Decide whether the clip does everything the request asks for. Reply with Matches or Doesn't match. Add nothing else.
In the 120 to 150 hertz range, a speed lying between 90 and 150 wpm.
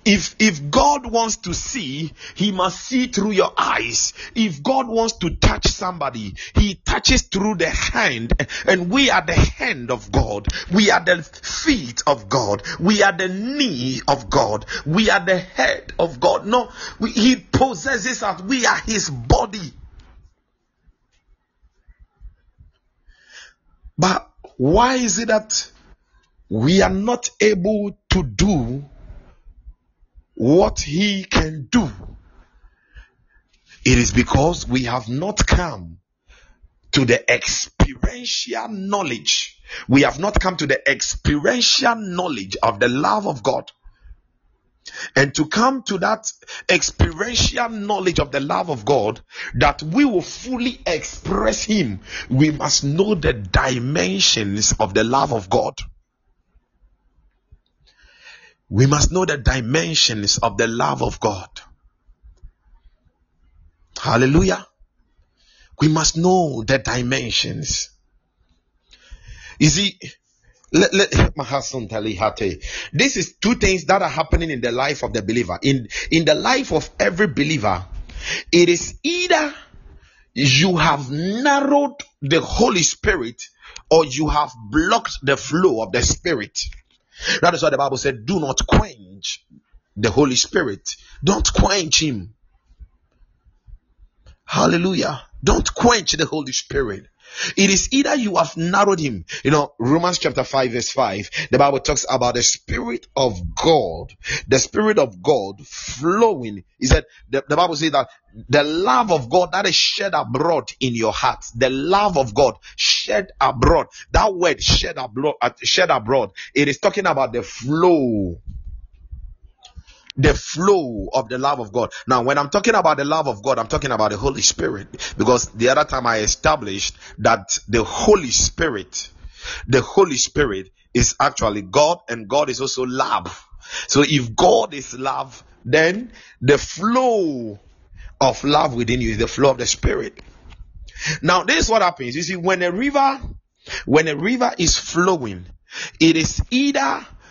Matches